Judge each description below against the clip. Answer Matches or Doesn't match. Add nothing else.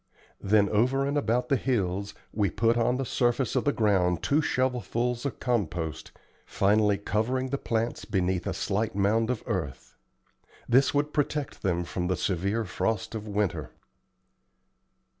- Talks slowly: Doesn't match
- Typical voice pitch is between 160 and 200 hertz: Doesn't match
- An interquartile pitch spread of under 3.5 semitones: Doesn't match